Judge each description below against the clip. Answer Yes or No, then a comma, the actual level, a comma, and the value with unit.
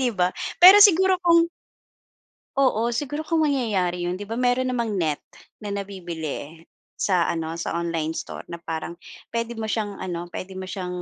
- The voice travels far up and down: Yes, wide, 6.2 semitones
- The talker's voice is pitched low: No, high, 200 Hz